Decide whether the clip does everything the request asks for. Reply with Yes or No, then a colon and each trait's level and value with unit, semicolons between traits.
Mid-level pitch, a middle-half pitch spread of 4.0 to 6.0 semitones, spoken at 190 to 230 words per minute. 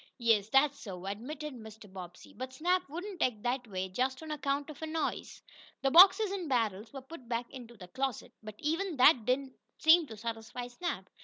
No: very high, 260 Hz; wide, 5.6 semitones; average, 200 wpm